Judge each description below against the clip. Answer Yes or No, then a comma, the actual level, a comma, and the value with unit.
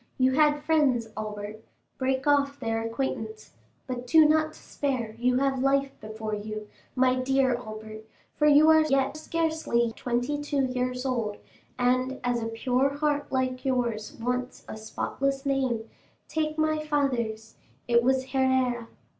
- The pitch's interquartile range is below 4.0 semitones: Yes, average, 3.2 semitones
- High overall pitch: Yes, very high, 255 Hz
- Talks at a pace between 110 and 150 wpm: Yes, average, 140 wpm